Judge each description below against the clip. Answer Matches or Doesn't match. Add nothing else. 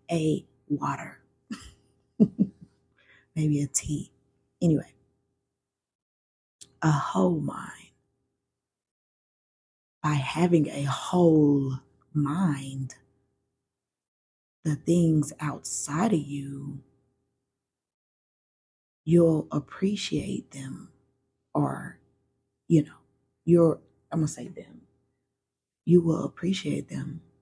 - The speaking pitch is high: Doesn't match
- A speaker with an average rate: Doesn't match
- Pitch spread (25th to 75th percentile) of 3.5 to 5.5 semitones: Doesn't match